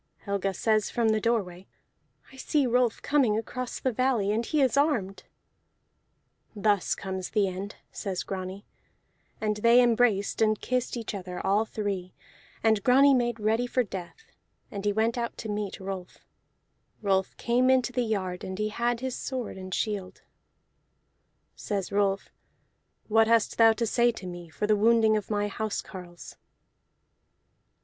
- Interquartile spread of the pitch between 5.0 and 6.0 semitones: No, average, 3.3 semitones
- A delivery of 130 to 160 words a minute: Yes, average, 155 wpm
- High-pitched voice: Yes, high, 215 Hz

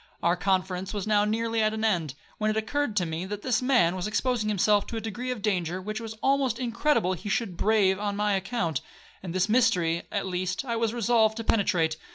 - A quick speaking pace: Yes, fast, 220 wpm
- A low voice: No, high, 210 Hz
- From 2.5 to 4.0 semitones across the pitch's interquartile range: Yes, average, 3.5 semitones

